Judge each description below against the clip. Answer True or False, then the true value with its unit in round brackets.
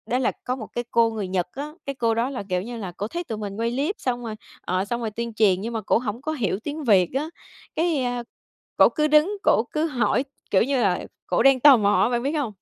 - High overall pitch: True (235 Hz)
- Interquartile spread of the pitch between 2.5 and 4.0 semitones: False (4.7 semitones)